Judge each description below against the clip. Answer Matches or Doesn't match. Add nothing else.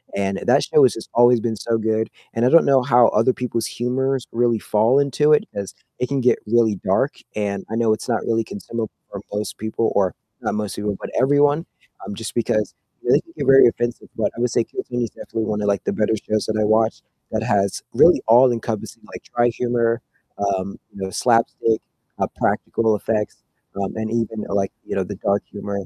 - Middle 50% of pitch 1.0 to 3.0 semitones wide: Matches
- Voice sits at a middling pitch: Doesn't match